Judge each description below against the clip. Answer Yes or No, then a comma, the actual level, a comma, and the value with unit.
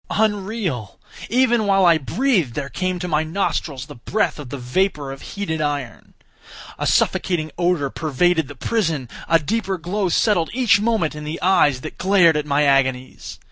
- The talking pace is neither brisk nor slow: Yes, average, 165 wpm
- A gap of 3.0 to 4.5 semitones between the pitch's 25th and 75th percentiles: No, wide, 5.5 semitones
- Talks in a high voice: No, medium, 165 Hz